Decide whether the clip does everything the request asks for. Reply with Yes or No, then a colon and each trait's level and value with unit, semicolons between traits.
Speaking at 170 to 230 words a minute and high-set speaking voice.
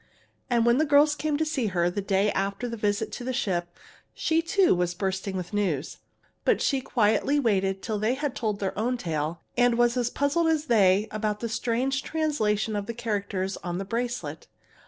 Yes: average, 200 wpm; high, 220 Hz